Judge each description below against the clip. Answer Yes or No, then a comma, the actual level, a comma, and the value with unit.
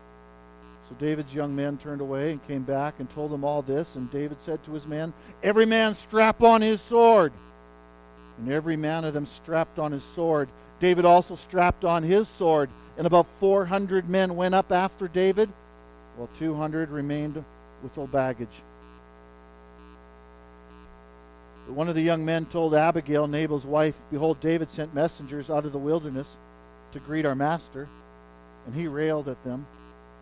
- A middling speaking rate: Yes, average, 165 wpm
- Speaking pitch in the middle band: Yes, medium, 150 Hz